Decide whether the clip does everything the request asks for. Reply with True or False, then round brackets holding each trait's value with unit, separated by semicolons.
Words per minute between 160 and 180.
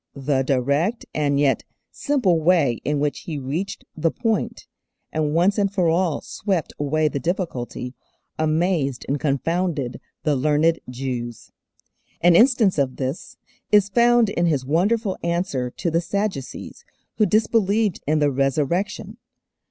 False (135 wpm)